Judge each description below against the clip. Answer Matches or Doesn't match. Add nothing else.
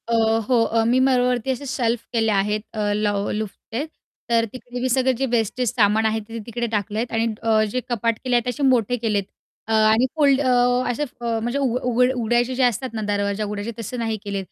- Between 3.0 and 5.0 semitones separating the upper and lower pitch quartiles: Doesn't match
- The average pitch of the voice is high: Matches